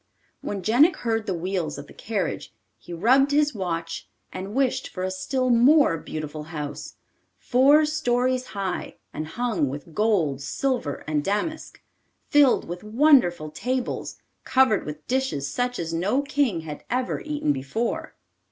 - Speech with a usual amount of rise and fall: No, wide, 7.9 semitones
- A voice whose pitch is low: No, high, 215 Hz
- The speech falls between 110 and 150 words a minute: Yes, average, 145 wpm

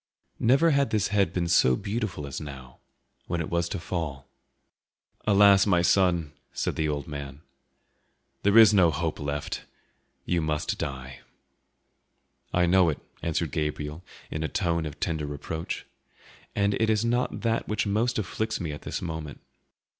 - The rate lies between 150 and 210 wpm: Yes, average, 160 wpm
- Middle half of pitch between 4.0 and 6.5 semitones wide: Yes, average, 5.2 semitones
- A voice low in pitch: Yes, very low, 85 Hz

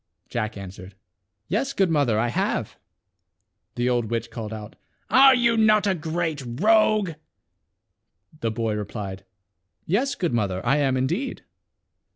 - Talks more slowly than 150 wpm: Yes, average, 140 wpm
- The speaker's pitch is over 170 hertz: No, low, 130 Hz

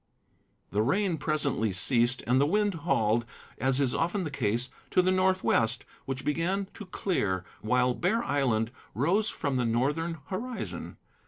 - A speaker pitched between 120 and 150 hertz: Yes, medium, 140 Hz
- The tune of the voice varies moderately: No, wide, 7.3 semitones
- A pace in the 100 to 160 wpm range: Yes, average, 150 wpm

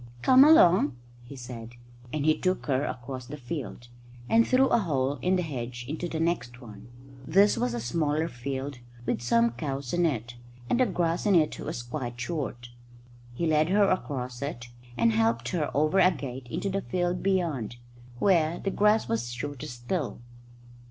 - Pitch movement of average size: No, wide, 6.3 semitones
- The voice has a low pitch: No, medium, 145 Hz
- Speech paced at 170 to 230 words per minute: Yes, average, 175 wpm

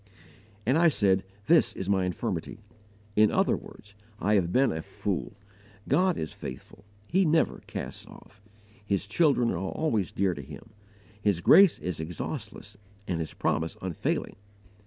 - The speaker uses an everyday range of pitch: No, wide, 7.3 semitones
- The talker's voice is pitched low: Yes, low, 100 Hz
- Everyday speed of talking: Yes, average, 150 wpm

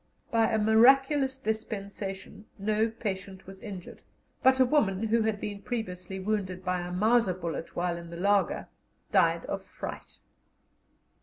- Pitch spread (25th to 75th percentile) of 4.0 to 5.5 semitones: No, average, 3.2 semitones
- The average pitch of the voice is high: Yes, high, 205 Hz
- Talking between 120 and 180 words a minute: Yes, average, 145 wpm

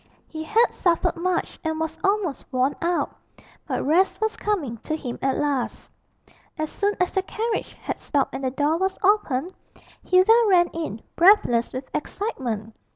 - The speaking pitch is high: Yes, very high, 330 Hz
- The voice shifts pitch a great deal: Yes, wide, 5.9 semitones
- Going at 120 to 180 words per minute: Yes, average, 160 wpm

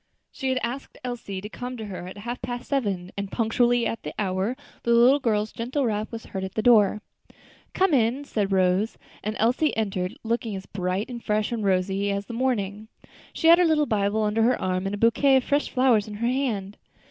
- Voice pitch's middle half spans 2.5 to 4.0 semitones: Yes, average, 3.6 semitones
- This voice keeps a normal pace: No, fast, 215 wpm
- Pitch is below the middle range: No, high, 220 Hz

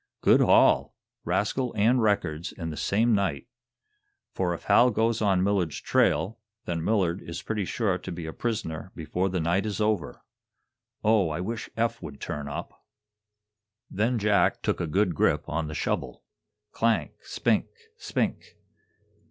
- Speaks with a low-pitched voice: Yes, very low, 95 Hz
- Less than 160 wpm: Yes, average, 150 wpm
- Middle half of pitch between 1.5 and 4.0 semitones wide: No, average, 4.7 semitones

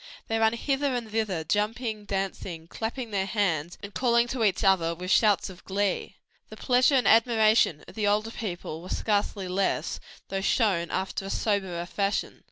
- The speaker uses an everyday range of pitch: Yes, average, 3.1 semitones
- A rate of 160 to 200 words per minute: Yes, average, 175 wpm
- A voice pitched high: Yes, high, 205 Hz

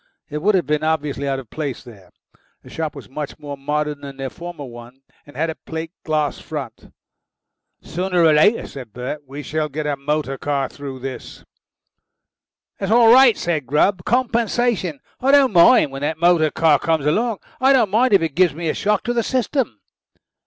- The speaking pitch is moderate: Yes, medium, 155 Hz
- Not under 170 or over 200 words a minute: Yes, average, 195 wpm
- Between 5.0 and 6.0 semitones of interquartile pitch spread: Yes, wide, 5.6 semitones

